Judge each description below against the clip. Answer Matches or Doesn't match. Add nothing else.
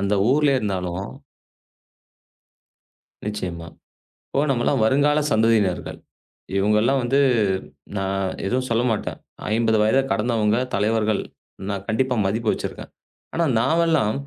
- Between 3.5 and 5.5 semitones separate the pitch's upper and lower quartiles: Matches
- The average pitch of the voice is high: Doesn't match